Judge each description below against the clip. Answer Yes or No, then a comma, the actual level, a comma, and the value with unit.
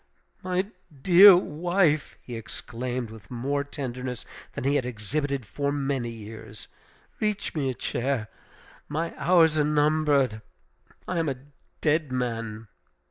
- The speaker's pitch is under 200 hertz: Yes, medium, 140 Hz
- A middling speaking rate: No, slow, 130 wpm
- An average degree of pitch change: Yes, average, 4.2 semitones